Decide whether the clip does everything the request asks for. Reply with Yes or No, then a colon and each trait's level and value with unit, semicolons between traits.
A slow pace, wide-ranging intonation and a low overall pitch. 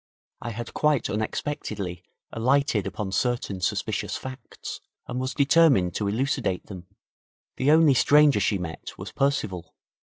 Yes: slow, 130 wpm; wide, 6.2 semitones; low, 120 Hz